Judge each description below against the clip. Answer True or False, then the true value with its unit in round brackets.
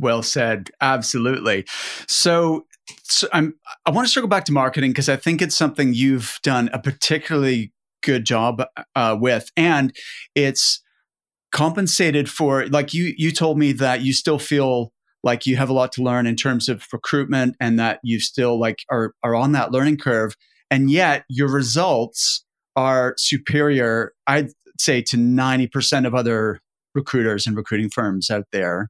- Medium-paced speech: True (165 wpm)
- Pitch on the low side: True (130 Hz)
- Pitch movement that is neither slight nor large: True (3.4 semitones)